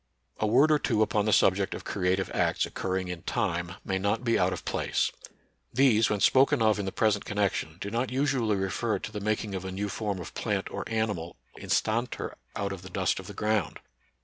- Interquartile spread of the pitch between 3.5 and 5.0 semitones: No, average, 2.9 semitones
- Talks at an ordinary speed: No, fast, 215 wpm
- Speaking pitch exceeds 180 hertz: No, low, 105 Hz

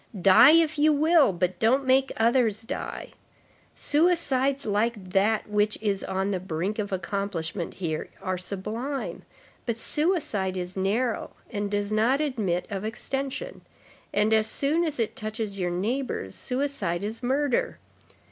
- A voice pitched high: Yes, high, 220 Hz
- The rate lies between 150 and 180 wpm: No, average, 140 wpm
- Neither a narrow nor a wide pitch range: No, wide, 5.8 semitones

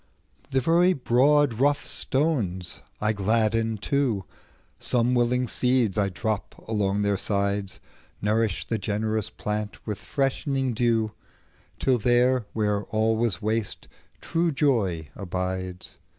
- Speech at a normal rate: No, slow, 110 wpm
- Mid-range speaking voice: No, low, 110 Hz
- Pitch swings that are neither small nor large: Yes, average, 3.7 semitones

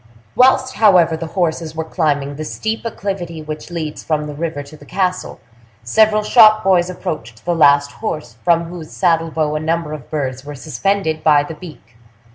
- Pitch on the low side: No, medium, 160 Hz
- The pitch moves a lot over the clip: No, average, 3.4 semitones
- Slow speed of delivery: No, average, 180 wpm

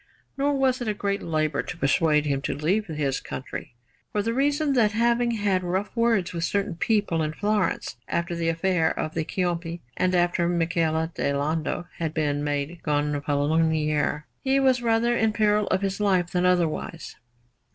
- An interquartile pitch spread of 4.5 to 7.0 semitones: Yes, average, 5.1 semitones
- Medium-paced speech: Yes, average, 170 wpm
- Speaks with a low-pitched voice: No, medium, 175 Hz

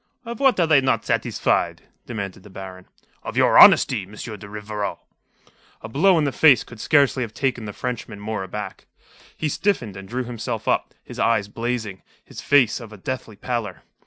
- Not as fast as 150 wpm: No, average, 185 wpm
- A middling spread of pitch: Yes, average, 4.3 semitones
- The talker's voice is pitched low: Yes, low, 115 Hz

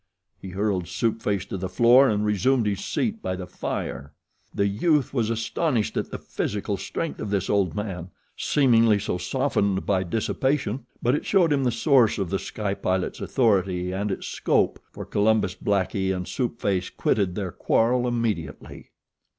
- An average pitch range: Yes, average, 4.2 semitones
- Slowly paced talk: No, average, 170 wpm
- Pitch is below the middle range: Yes, low, 105 Hz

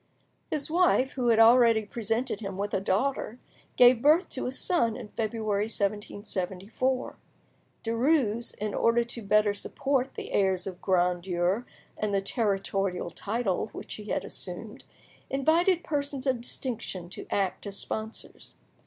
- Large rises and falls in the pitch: No, average, 4.3 semitones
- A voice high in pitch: Yes, high, 220 Hz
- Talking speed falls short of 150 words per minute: Yes, average, 140 wpm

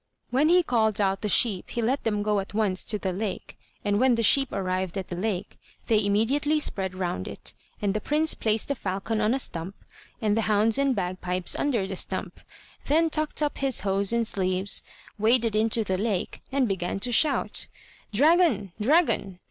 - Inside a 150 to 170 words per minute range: No, average, 190 wpm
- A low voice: No, high, 215 Hz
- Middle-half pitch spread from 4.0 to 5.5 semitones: Yes, average, 4.7 semitones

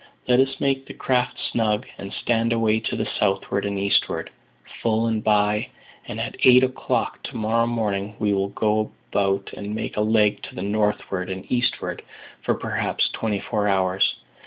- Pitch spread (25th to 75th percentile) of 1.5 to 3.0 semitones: Yes, narrow, 2.5 semitones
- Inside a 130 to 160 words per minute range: No, average, 175 wpm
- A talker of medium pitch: No, low, 105 Hz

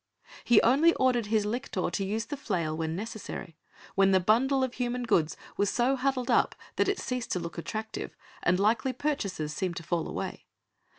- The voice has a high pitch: Yes, high, 220 Hz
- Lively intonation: Yes, wide, 5.7 semitones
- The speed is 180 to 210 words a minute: Yes, average, 185 wpm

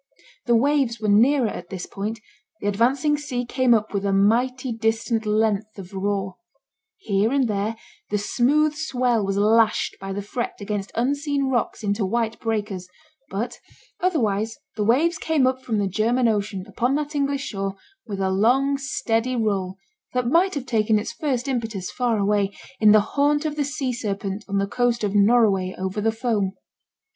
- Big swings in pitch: No, average, 4.1 semitones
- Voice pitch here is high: Yes, high, 225 Hz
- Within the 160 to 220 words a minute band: Yes, average, 175 wpm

